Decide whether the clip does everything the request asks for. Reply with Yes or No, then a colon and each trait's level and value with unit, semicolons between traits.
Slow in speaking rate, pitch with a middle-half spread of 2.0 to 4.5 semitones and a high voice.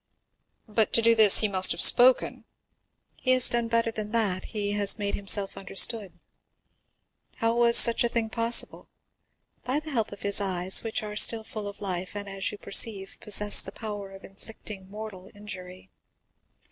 No: average, 170 wpm; average, 2.7 semitones; high, 210 Hz